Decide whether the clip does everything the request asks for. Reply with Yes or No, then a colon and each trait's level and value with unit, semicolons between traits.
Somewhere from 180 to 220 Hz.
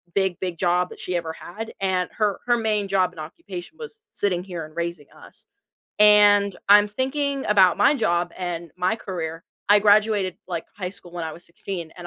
Yes: medium, 185 Hz